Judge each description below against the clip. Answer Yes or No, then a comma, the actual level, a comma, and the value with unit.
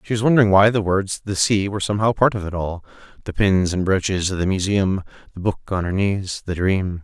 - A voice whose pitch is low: Yes, very low, 95 Hz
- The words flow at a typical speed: No, fast, 230 wpm